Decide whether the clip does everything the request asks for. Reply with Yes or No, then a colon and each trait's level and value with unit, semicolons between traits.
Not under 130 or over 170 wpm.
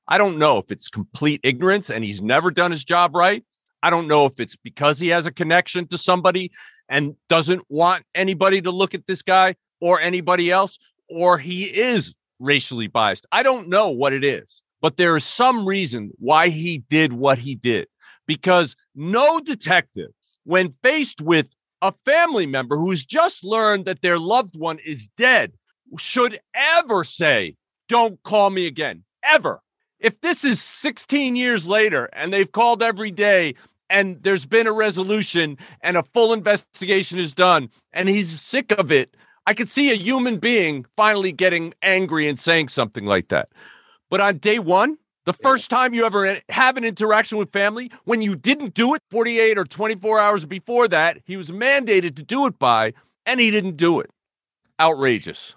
No: average, 180 wpm